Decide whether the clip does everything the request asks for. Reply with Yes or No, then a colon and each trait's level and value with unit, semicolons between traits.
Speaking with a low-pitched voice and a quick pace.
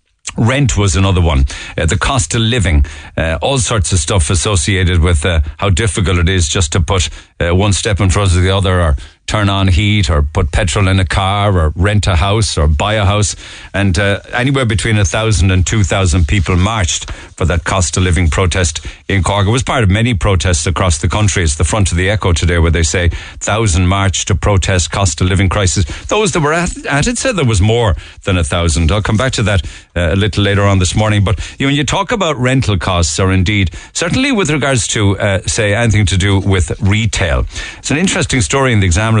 Yes: very low, 95 Hz; fast, 230 wpm